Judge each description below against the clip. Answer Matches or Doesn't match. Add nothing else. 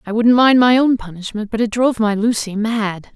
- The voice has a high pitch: Matches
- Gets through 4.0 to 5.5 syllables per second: Matches